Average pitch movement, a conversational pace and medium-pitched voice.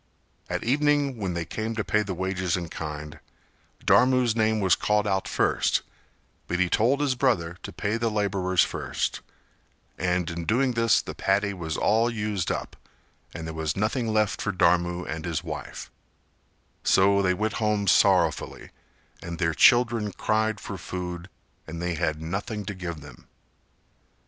No: average, 4.0 semitones; average, 160 wpm; very low, 95 Hz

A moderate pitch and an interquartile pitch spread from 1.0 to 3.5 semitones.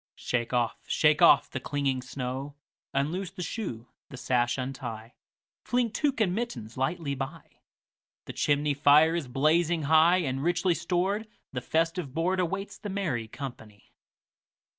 No: medium, 145 Hz; wide, 5.5 semitones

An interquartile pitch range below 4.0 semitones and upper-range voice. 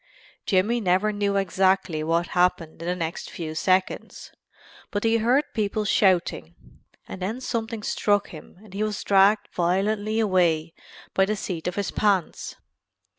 Yes: average, 3.1 semitones; high, 195 Hz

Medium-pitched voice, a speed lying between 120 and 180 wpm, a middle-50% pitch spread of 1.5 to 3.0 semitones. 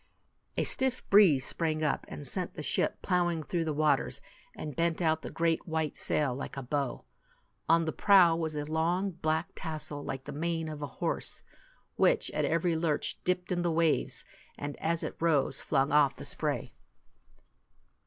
Yes: medium, 160 Hz; average, 175 wpm; narrow, 2.4 semitones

